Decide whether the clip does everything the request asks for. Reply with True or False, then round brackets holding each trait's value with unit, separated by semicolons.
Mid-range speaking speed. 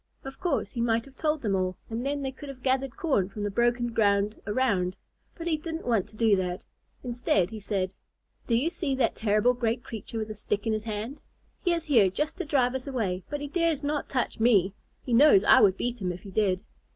False (235 wpm)